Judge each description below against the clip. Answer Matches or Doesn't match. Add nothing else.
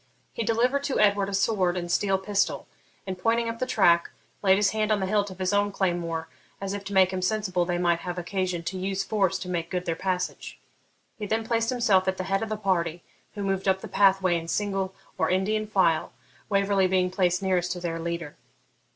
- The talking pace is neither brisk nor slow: Doesn't match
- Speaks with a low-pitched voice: Doesn't match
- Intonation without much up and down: Matches